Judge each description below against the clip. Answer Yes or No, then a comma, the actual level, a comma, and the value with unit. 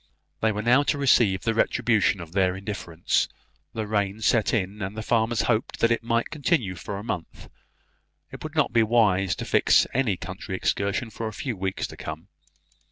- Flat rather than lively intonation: No, average, 3.4 semitones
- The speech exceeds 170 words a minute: Yes, average, 190 wpm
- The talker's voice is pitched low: Yes, low, 105 Hz